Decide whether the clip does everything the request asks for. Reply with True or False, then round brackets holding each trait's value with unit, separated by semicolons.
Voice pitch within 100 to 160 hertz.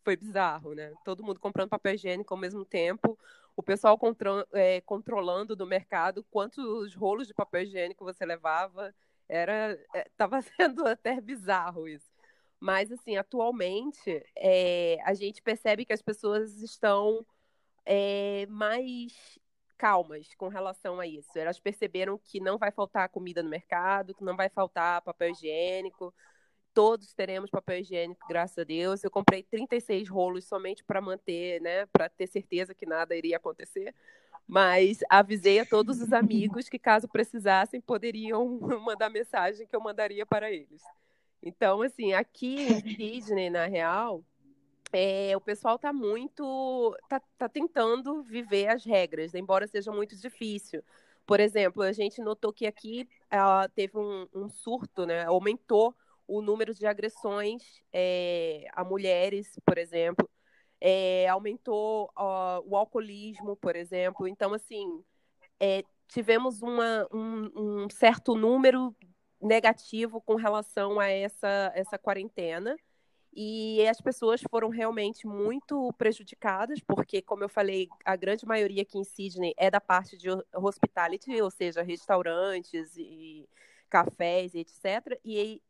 False (205 Hz)